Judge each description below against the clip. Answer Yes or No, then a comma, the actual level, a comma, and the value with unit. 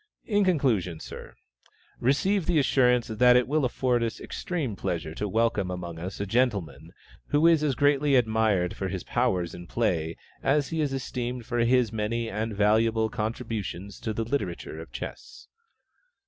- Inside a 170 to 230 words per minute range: No, average, 160 wpm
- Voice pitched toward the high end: No, low, 115 Hz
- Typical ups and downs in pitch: Yes, average, 4.7 semitones